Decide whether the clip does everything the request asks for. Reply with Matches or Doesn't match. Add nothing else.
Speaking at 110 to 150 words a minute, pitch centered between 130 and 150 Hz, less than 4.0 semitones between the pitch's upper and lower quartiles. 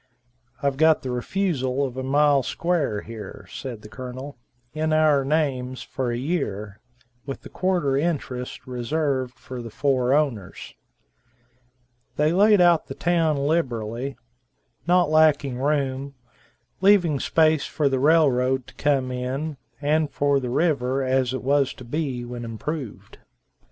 Matches